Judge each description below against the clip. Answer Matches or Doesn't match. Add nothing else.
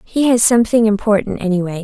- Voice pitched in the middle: Doesn't match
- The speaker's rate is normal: Matches